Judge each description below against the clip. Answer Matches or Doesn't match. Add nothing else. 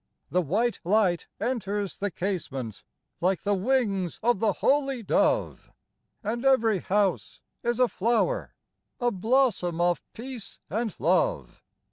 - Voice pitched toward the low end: Doesn't match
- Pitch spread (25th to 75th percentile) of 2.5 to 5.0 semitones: Matches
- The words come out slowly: Matches